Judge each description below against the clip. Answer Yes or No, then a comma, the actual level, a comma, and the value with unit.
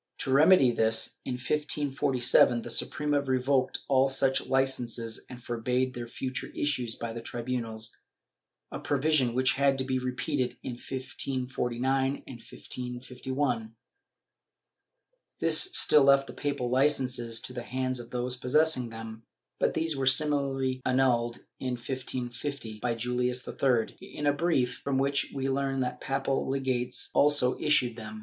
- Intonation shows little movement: Yes, narrow, 2.0 semitones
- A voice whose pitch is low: Yes, low, 130 Hz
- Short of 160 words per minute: Yes, average, 140 wpm